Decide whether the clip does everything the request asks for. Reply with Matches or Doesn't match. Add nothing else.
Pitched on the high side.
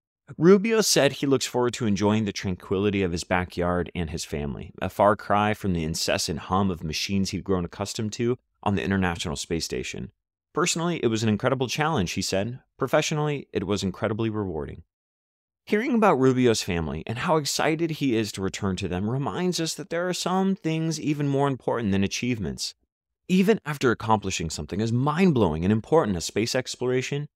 Doesn't match